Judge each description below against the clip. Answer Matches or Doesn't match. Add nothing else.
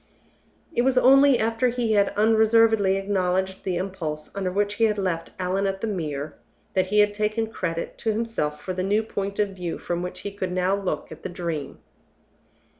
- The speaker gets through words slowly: Doesn't match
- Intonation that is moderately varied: Matches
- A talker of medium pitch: Doesn't match